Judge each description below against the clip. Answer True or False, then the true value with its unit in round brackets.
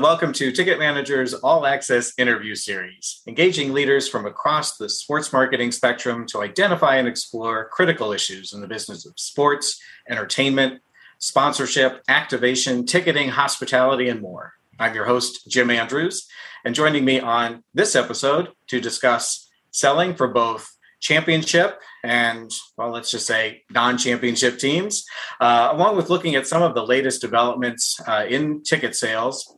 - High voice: False (130 Hz)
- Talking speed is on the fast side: False (150 wpm)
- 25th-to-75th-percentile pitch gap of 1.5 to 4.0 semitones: True (3.4 semitones)